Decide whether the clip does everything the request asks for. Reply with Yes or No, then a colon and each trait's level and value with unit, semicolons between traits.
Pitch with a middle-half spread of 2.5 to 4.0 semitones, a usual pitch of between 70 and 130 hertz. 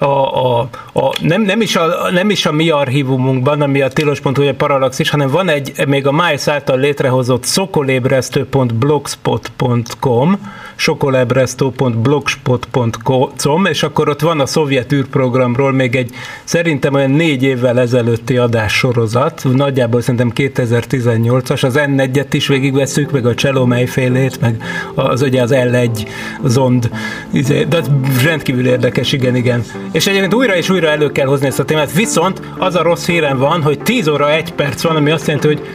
No: average, 2.9 semitones; medium, 140 Hz